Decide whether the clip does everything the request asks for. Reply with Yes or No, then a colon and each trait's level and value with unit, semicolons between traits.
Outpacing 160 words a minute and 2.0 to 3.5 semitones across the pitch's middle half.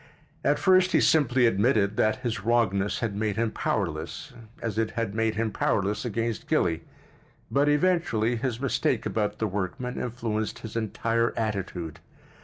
No: average, 140 wpm; average, 2.8 semitones